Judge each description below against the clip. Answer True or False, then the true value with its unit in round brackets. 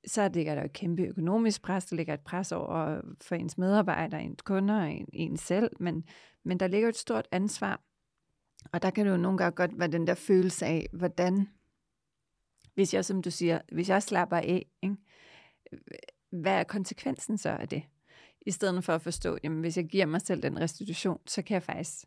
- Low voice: False (180 Hz)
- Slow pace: False (210 wpm)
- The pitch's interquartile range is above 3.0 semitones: False (2.7 semitones)